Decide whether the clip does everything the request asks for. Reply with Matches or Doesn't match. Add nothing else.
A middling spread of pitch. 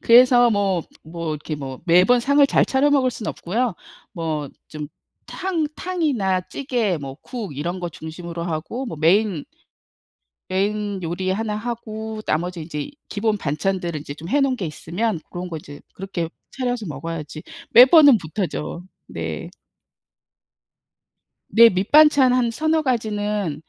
Doesn't match